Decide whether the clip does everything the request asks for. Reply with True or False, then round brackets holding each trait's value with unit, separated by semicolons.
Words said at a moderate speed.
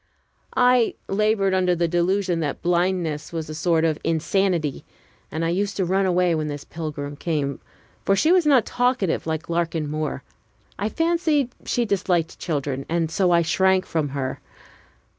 True (160 wpm)